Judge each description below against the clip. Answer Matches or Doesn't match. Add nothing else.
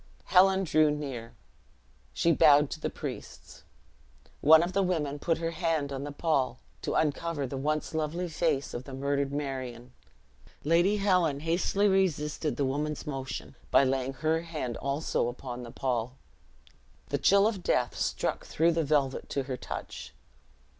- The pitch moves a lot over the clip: Doesn't match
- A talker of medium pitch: Matches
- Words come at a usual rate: Matches